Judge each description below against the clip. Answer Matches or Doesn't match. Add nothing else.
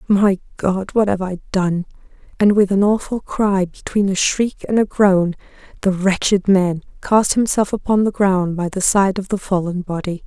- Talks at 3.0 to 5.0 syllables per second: Matches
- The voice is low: Doesn't match